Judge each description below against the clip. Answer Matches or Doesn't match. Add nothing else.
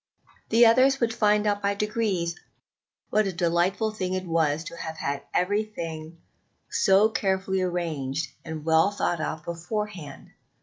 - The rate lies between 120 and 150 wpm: Matches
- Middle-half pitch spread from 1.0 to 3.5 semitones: Doesn't match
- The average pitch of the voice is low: Doesn't match